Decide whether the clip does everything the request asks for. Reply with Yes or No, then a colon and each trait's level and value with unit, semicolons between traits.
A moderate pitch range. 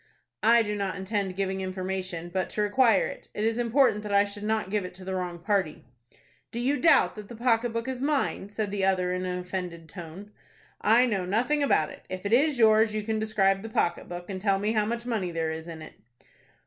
Yes: average, 3.4 semitones